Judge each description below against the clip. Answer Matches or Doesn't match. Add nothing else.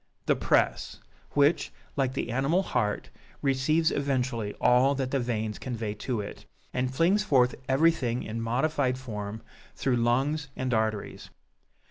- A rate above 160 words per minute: Doesn't match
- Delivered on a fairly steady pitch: Doesn't match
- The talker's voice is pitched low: Matches